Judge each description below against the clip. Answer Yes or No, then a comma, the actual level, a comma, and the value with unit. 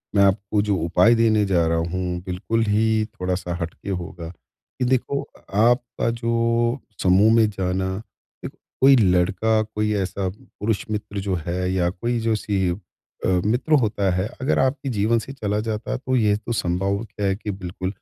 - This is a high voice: No, low, 105 Hz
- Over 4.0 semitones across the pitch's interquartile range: No, average, 3.7 semitones